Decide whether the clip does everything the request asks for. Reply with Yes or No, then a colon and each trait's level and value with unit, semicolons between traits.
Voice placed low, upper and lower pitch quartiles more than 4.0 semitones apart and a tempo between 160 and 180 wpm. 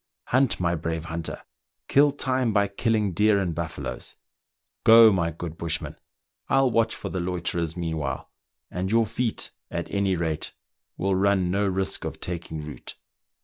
No: very low, 95 Hz; average, 4.7 semitones; average, 150 wpm